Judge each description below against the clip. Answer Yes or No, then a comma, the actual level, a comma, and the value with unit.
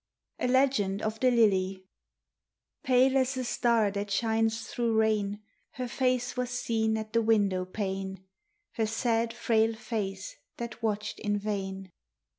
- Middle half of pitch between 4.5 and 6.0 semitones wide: No, average, 2.8 semitones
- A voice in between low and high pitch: No, high, 220 Hz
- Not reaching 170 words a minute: Yes, average, 140 wpm